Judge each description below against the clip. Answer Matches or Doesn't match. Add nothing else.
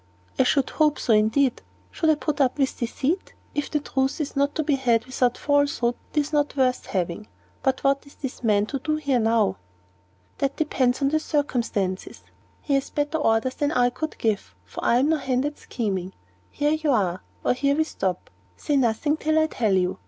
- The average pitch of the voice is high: Matches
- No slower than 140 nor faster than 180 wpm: Doesn't match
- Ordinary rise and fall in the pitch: Matches